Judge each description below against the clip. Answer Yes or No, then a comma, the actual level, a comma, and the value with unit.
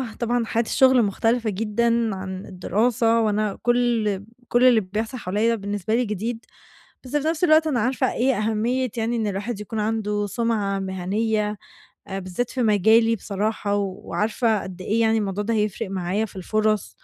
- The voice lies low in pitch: No, high, 220 Hz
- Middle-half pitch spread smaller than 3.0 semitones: Yes, narrow, 2.5 semitones